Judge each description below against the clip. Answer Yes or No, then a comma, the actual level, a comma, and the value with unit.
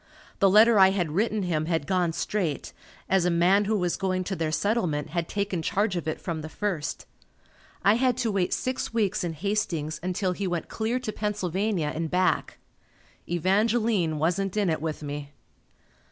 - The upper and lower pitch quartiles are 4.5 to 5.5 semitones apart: No, average, 4.1 semitones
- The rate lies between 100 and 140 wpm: No, average, 180 wpm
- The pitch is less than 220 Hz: Yes, medium, 185 Hz